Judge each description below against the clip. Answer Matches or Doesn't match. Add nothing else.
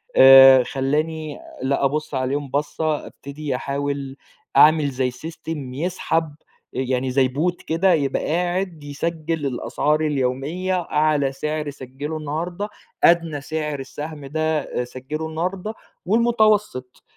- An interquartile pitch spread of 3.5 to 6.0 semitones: Doesn't match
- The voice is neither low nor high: Matches